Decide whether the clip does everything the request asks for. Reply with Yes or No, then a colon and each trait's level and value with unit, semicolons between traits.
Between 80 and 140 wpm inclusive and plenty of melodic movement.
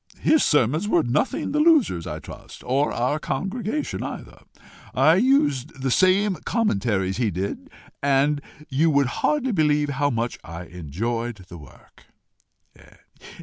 Yes: slow, 135 wpm; wide, 8.2 semitones